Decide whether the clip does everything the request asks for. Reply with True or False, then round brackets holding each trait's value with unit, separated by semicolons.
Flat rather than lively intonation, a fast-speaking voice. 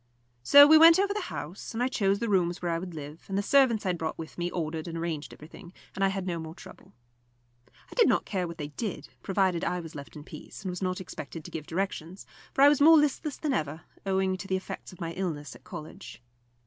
False (3.9 semitones; 250 wpm)